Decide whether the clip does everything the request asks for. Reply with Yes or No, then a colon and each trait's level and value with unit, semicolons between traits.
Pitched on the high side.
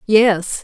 Yes: high, 205 Hz